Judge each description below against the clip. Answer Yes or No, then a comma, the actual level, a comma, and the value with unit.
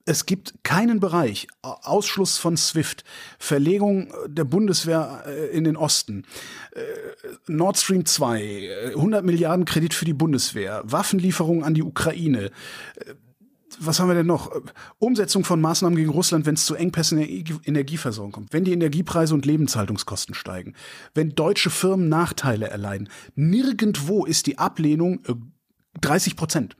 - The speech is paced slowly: No, average, 135 wpm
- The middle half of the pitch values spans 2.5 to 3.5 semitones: No, average, 4.3 semitones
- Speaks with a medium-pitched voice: Yes, medium, 165 Hz